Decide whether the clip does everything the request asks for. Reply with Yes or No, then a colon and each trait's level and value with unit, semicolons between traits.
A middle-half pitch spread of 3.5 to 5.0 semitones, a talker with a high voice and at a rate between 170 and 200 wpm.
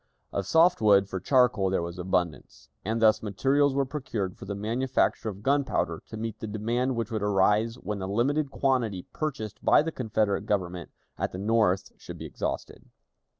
No: average, 4.4 semitones; low, 110 Hz; average, 180 wpm